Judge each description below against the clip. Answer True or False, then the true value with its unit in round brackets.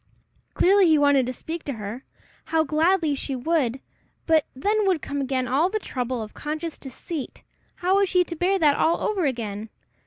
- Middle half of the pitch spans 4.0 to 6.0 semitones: True (5.4 semitones)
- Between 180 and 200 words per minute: True (185 wpm)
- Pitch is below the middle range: False (305 Hz)